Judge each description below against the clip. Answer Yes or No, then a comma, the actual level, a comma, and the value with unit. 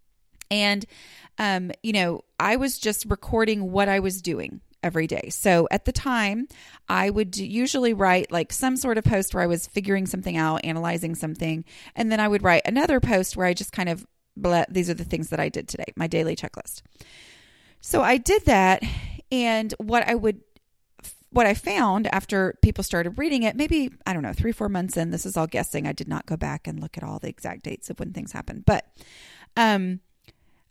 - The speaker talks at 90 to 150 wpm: No, fast, 205 wpm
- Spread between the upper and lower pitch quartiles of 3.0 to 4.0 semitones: No, average, 4.6 semitones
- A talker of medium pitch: No, high, 195 Hz